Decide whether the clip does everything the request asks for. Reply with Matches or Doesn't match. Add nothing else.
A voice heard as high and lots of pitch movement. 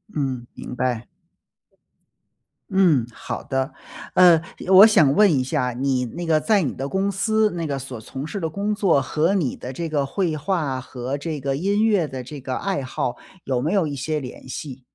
Doesn't match